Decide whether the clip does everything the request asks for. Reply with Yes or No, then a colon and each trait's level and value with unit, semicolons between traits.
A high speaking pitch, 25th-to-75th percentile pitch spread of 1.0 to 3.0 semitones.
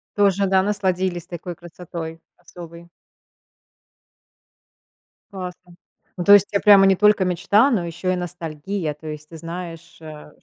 No: medium, 180 Hz; average, 2.7 semitones